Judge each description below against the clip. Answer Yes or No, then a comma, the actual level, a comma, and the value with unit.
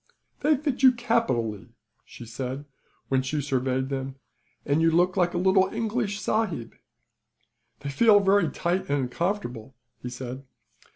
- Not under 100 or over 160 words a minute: Yes, average, 140 wpm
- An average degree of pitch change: No, wide, 7.6 semitones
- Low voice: No, medium, 160 Hz